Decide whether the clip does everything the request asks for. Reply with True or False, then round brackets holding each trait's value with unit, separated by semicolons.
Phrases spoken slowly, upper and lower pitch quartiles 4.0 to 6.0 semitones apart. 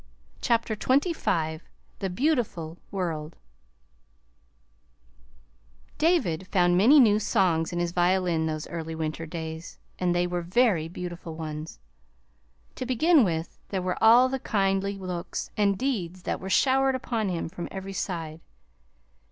True (130 wpm; 5.0 semitones)